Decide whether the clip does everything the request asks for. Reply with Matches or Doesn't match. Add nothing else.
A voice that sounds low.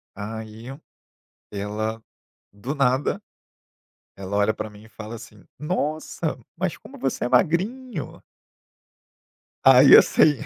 Matches